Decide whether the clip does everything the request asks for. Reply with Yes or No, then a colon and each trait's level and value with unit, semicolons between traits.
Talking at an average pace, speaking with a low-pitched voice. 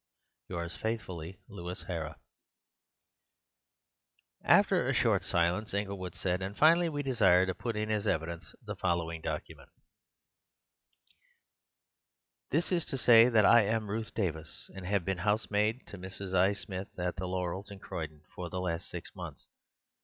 Yes: average, 150 wpm; very low, 95 Hz